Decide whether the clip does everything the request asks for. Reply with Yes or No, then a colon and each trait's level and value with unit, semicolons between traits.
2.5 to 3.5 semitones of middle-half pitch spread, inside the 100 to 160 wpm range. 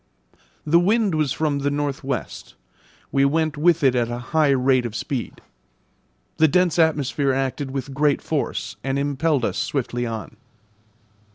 Yes: average, 2.9 semitones; average, 155 wpm